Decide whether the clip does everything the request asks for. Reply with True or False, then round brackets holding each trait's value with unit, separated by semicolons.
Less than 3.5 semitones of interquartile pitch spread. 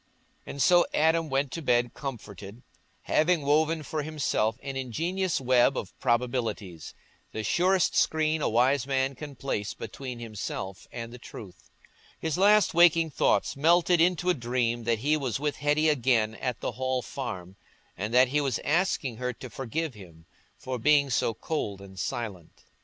False (5.0 semitones)